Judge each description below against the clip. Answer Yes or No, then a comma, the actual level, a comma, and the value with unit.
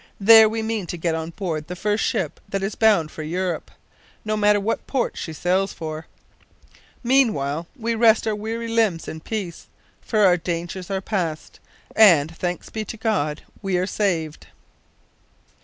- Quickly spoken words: No, average, 165 wpm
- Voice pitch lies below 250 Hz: Yes, high, 190 Hz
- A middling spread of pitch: Yes, average, 4.8 semitones